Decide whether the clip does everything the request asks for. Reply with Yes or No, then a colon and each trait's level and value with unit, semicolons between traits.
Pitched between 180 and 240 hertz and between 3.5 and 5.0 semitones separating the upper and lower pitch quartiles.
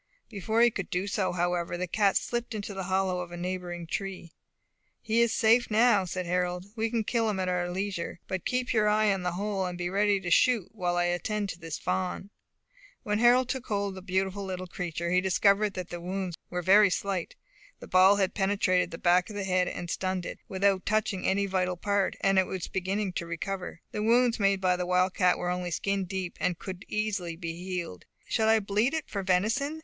No: high, 190 Hz; narrow, 2.6 semitones